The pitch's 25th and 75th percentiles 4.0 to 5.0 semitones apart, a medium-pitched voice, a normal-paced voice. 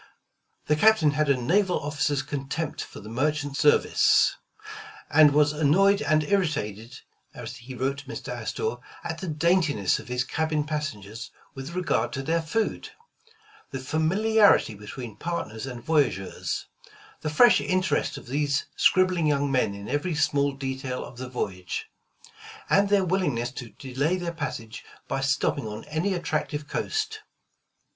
Yes: average, 4.6 semitones; medium, 145 Hz; average, 150 wpm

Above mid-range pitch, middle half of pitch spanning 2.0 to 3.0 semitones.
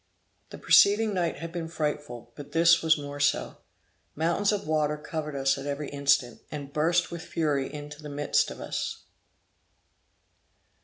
No: medium, 150 Hz; narrow, 2.6 semitones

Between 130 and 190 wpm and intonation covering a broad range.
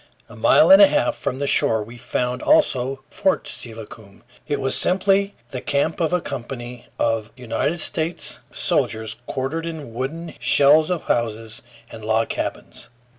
Yes: average, 155 wpm; wide, 6.0 semitones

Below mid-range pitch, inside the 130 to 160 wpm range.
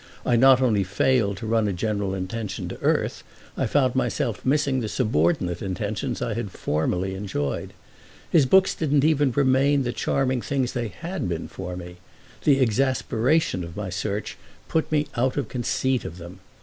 No: low, 115 Hz; average, 170 wpm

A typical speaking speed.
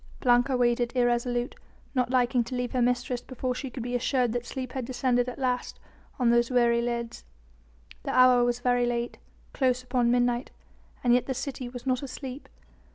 Yes: average, 180 wpm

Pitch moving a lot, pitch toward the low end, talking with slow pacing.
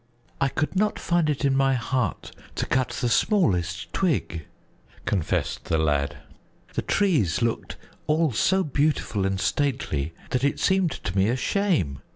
No: wide, 8.7 semitones; low, 130 Hz; average, 155 wpm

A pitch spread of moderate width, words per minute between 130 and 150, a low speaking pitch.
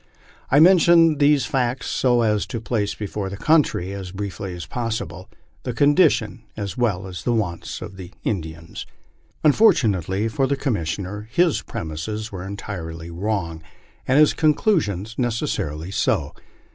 No: wide, 6.1 semitones; average, 140 wpm; low, 105 Hz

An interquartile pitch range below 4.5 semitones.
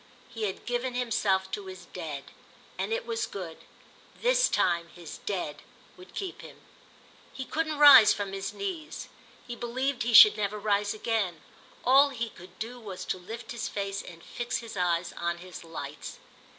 No: average, 5.1 semitones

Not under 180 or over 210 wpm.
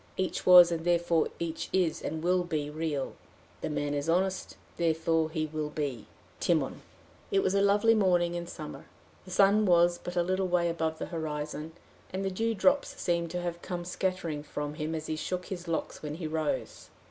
Yes: average, 195 wpm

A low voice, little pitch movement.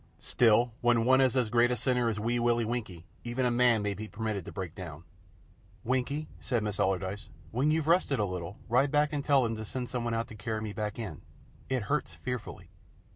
No: low, 120 Hz; average, 3.2 semitones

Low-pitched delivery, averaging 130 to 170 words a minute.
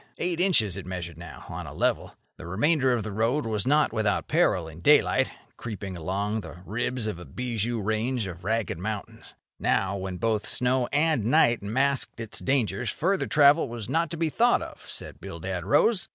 No: low, 115 Hz; average, 185 wpm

